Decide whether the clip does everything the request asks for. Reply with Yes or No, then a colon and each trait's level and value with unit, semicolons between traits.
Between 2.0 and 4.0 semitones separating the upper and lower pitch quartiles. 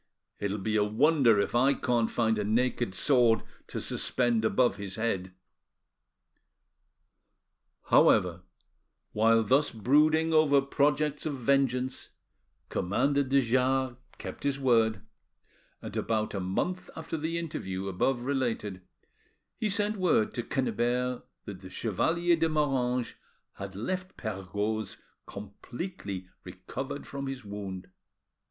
No: average, 5.2 semitones